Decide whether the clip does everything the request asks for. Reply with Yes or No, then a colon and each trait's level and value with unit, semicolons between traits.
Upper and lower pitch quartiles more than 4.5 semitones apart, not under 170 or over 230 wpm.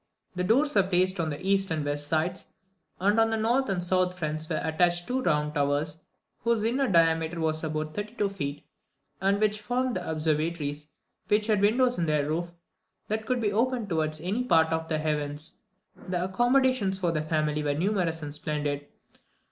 Yes: average, 5.2 semitones; average, 185 wpm